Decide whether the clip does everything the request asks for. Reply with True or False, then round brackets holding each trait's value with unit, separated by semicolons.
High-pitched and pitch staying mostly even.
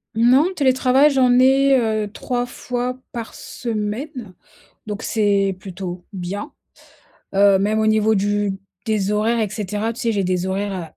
False (215 Hz; 3.6 semitones)